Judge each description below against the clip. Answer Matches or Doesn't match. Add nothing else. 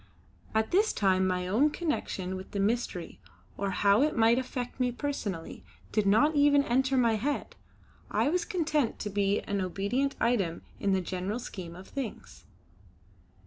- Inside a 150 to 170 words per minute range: Matches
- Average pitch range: Doesn't match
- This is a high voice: Matches